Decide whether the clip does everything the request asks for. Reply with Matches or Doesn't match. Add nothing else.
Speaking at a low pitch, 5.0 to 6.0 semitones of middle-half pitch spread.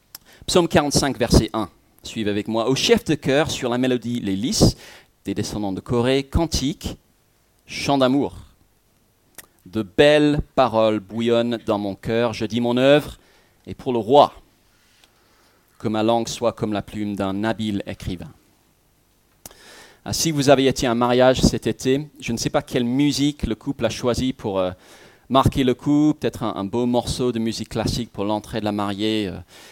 Doesn't match